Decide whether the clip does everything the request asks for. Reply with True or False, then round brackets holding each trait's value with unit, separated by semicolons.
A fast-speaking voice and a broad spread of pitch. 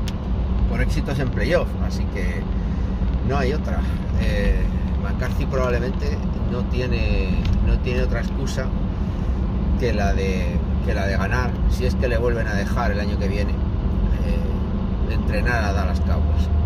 False (155 wpm; 5.9 semitones)